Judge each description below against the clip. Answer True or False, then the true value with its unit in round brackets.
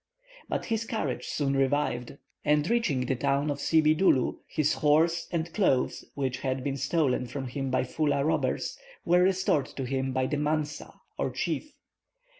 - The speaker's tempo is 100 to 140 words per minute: False (160 wpm)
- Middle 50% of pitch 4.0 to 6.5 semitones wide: False (3.2 semitones)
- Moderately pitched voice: True (145 Hz)